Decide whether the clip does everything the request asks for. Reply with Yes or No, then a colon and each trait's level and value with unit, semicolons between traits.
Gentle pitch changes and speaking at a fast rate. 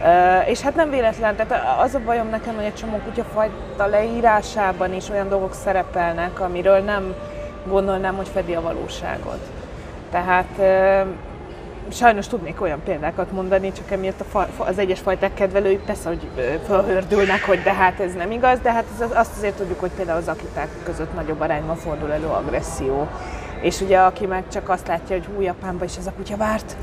Yes: narrow, 2.3 semitones; fast, 175 wpm